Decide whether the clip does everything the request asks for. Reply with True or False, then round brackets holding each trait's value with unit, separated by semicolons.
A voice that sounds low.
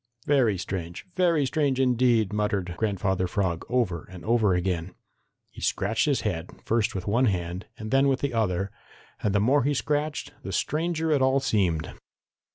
True (110 Hz)